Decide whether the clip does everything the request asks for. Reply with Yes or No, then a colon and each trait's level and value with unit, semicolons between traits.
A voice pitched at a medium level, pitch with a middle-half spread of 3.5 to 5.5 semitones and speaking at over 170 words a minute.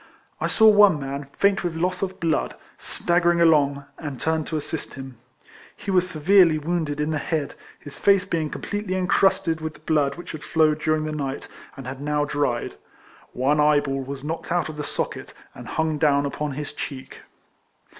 No: medium, 155 Hz; average, 3.0 semitones; average, 185 wpm